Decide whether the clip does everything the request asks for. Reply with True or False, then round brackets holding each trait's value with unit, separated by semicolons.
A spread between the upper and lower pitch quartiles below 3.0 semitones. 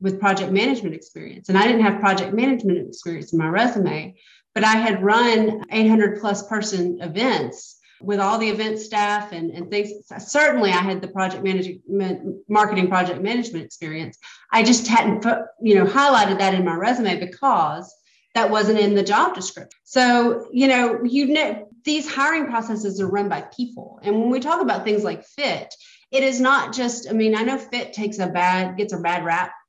False (3.7 semitones)